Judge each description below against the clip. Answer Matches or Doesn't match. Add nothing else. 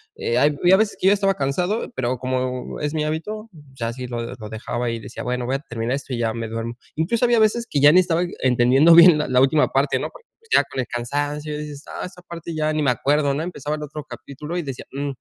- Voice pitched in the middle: Matches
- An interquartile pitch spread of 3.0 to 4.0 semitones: Doesn't match